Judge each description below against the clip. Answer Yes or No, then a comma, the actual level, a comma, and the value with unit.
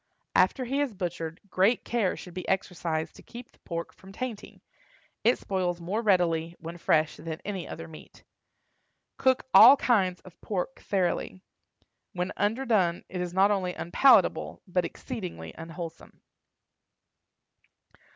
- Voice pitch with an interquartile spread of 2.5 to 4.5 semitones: Yes, average, 3.6 semitones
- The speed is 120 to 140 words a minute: Yes, slow, 135 wpm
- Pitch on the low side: No, medium, 185 Hz